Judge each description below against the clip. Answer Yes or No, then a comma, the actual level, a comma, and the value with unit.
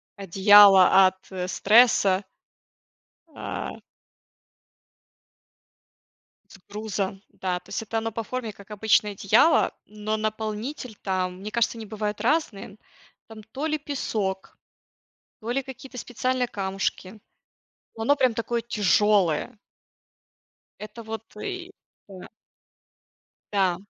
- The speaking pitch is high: Yes, high, 215 Hz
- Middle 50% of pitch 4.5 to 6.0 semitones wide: No, average, 3.2 semitones